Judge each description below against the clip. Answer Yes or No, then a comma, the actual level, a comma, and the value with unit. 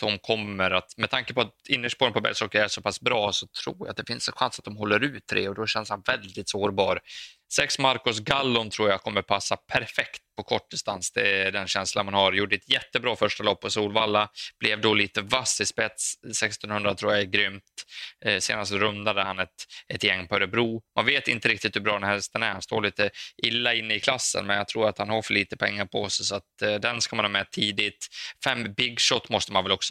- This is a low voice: Yes, low, 105 Hz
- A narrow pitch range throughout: Yes, narrow, 1.8 semitones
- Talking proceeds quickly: Yes, fast, 245 wpm